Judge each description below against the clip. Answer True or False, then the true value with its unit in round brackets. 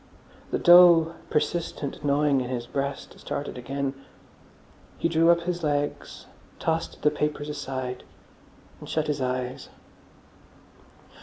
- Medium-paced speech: False (120 wpm)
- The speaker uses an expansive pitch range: False (3.3 semitones)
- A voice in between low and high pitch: True (145 Hz)